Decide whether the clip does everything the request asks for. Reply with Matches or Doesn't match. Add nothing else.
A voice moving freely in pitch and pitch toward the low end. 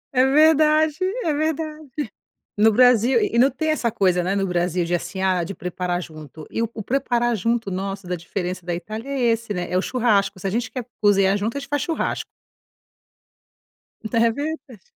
Doesn't match